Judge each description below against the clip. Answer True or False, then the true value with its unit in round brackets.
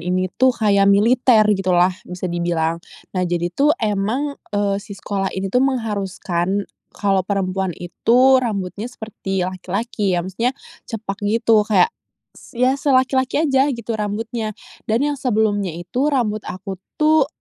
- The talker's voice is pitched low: False (210 Hz)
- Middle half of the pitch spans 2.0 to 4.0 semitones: False (4.5 semitones)